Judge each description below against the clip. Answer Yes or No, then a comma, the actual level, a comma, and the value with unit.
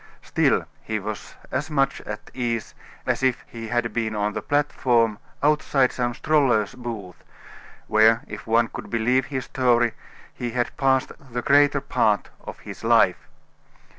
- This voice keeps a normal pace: Yes, average, 150 wpm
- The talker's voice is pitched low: Yes, low, 120 Hz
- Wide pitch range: No, average, 3.0 semitones